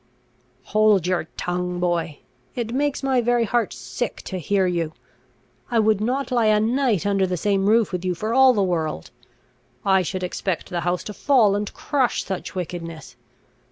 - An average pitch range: Yes, average, 4.5 semitones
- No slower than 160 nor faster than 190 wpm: Yes, average, 175 wpm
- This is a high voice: Yes, high, 200 Hz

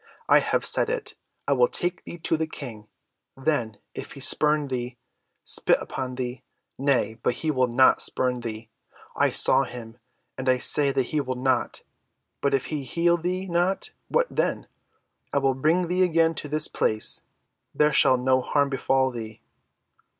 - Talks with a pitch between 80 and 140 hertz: Yes, low, 135 Hz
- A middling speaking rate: Yes, average, 165 wpm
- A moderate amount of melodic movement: Yes, average, 4.1 semitones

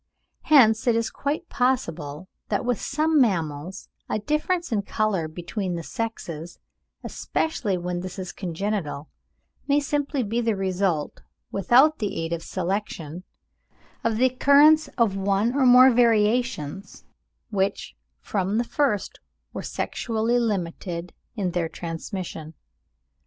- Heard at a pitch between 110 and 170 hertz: No, high, 205 Hz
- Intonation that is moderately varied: No, wide, 5.7 semitones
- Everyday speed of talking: No, slow, 125 wpm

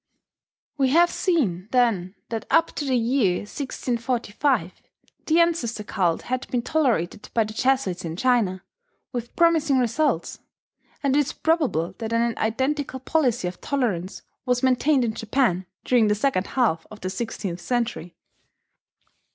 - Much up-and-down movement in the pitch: No, average, 4.8 semitones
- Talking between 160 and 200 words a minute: No, average, 145 wpm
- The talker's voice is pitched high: Yes, high, 240 Hz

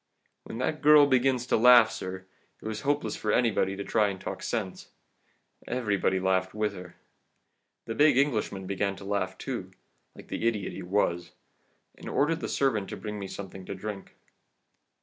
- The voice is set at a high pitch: No, low, 105 Hz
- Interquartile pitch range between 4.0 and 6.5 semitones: Yes, average, 4.4 semitones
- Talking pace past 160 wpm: Yes, average, 170 wpm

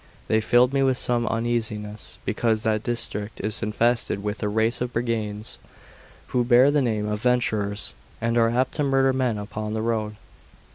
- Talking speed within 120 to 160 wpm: No, average, 175 wpm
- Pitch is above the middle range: No, low, 115 Hz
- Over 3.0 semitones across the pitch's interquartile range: No, narrow, 2.4 semitones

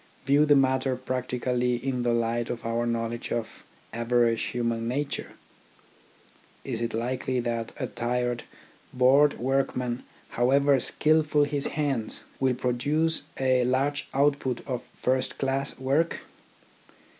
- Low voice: Yes, low, 125 Hz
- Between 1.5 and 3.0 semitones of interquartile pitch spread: Yes, narrow, 2.4 semitones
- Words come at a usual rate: No, slow, 120 wpm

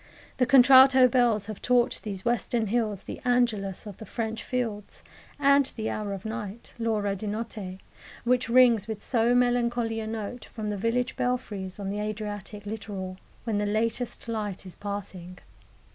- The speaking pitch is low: No, high, 220 Hz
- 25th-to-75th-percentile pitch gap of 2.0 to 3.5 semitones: Yes, average, 3.0 semitones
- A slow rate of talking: No, average, 160 wpm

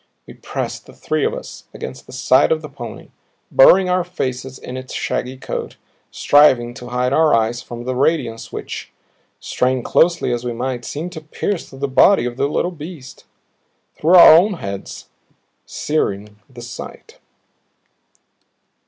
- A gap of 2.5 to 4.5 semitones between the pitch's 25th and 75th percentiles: No, wide, 5.4 semitones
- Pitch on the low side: Yes, low, 130 Hz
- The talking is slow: No, average, 160 wpm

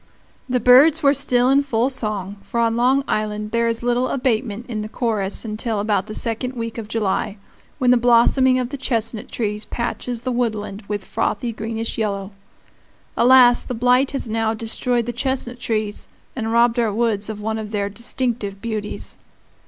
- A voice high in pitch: Yes, high, 230 Hz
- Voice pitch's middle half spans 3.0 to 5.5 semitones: No, narrow, 2.6 semitones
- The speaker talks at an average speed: Yes, average, 180 wpm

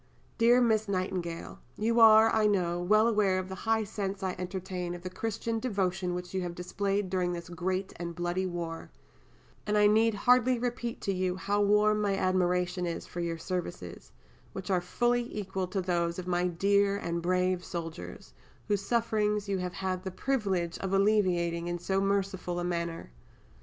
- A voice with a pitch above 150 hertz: Yes, high, 190 Hz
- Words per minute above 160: Yes, average, 180 wpm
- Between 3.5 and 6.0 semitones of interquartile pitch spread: No, average, 2.9 semitones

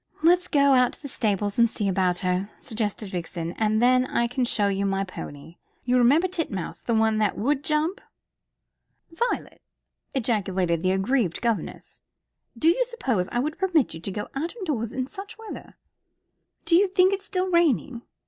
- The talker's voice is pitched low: No, high, 240 Hz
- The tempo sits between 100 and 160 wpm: No, average, 175 wpm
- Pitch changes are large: Yes, wide, 8.2 semitones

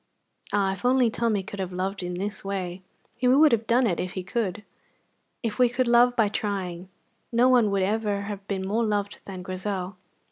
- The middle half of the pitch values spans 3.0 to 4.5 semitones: Yes, average, 3.6 semitones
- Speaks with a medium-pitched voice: No, high, 205 Hz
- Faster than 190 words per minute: Yes, average, 200 wpm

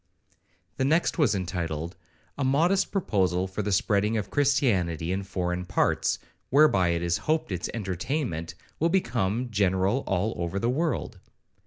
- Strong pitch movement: Yes, wide, 6.8 semitones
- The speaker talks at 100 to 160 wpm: Yes, average, 145 wpm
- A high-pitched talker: No, low, 100 Hz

